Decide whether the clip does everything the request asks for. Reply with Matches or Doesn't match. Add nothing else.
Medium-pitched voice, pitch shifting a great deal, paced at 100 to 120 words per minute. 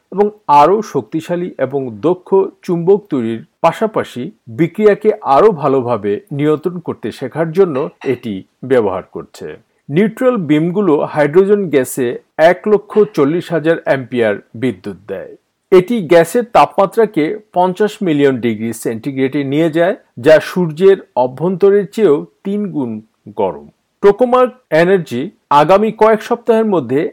Matches